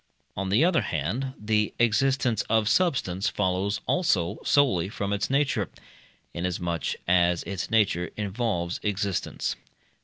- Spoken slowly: Yes, slow, 120 wpm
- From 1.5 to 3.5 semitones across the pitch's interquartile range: No, average, 4.7 semitones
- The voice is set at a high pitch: No, low, 100 Hz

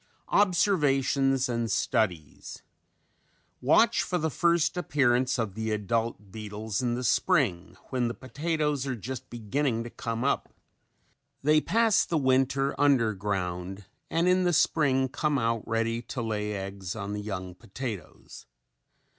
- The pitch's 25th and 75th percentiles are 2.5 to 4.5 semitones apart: No, average, 5.2 semitones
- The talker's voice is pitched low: Yes, low, 120 Hz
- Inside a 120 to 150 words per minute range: Yes, average, 140 wpm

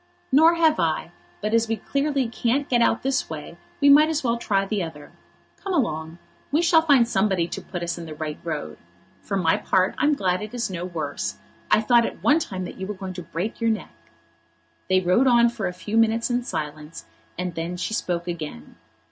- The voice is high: Yes, high, 200 Hz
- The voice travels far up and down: Yes, wide, 6.0 semitones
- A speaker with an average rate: No, fast, 215 wpm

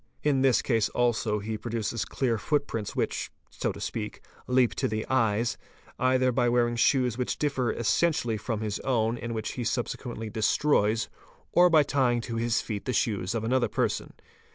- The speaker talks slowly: No, average, 175 wpm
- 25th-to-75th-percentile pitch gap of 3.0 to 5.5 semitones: No, narrow, 2.6 semitones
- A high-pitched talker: No, low, 120 Hz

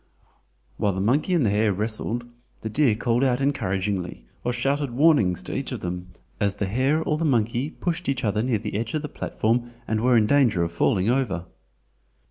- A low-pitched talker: Yes, low, 115 Hz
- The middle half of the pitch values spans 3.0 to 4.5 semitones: No, average, 5.0 semitones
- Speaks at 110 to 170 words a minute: No, average, 200 wpm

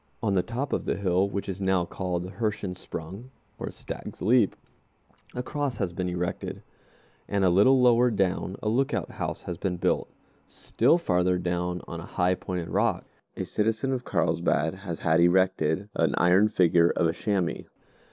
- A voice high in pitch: No, very low, 95 Hz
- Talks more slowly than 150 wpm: No, average, 170 wpm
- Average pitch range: Yes, average, 3.3 semitones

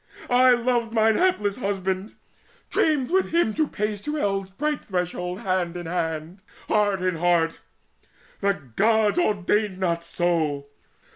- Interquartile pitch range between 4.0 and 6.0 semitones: Yes, average, 4.4 semitones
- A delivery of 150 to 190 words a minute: No, average, 140 wpm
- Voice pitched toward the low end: No, high, 195 Hz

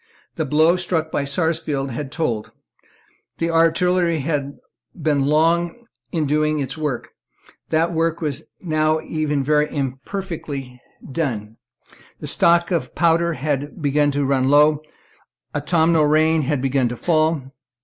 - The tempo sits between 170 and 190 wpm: No, slow, 135 wpm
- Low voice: No, medium, 155 Hz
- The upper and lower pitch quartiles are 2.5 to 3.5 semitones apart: Yes, average, 2.9 semitones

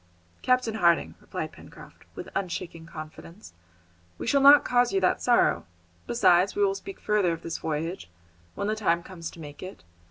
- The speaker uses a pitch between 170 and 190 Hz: Yes, medium, 185 Hz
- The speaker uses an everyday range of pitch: No, wide, 6.4 semitones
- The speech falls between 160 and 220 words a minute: Yes, average, 170 wpm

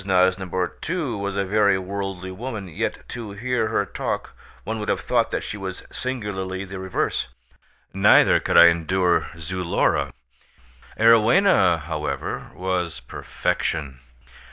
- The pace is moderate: No, slow, 130 wpm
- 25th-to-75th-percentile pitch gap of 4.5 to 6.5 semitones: No, average, 2.8 semitones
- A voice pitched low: Yes, very low, 95 Hz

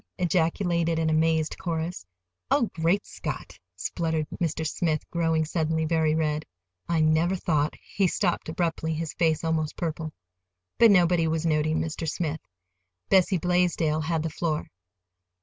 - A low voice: No, medium, 160 Hz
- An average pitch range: No, narrow, 1.5 semitones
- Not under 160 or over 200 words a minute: No, slow, 135 wpm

